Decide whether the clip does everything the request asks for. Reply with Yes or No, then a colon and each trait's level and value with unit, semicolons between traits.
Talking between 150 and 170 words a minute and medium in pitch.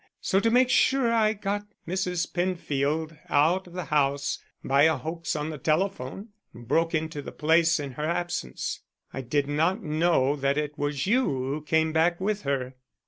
No: average, 180 wpm; medium, 160 Hz